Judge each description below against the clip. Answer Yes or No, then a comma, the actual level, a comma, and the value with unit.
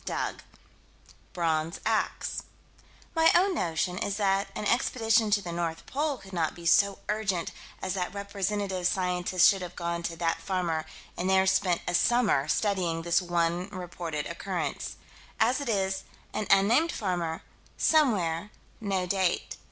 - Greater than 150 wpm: No, average, 145 wpm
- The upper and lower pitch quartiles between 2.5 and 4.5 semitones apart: Yes, average, 3.1 semitones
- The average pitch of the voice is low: No, medium, 185 Hz